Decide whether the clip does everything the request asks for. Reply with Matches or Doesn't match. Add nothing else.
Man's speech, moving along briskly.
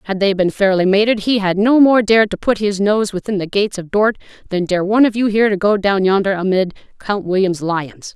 Doesn't match